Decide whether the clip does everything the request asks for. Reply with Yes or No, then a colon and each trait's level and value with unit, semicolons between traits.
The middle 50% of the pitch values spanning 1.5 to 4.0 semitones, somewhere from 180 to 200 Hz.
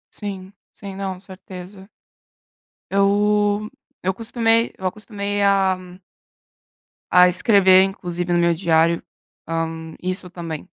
Yes: narrow, 2.4 semitones; high, 190 Hz